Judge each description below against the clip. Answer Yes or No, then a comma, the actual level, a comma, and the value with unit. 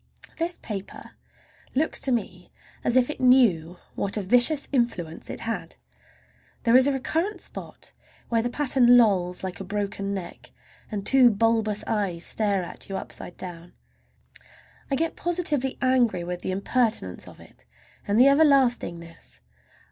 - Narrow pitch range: No, wide, 5.5 semitones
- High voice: Yes, high, 225 Hz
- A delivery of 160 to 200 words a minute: No, average, 150 wpm